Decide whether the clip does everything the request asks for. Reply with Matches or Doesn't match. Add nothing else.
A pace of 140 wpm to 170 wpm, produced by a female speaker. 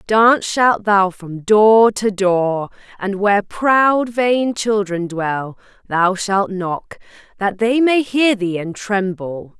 Matches